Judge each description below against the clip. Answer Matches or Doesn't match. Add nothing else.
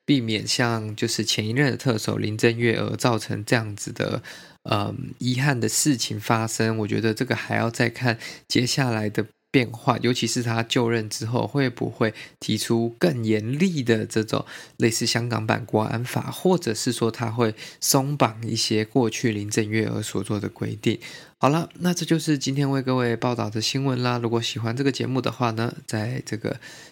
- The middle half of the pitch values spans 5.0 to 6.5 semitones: Doesn't match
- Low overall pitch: Matches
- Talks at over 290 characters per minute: Doesn't match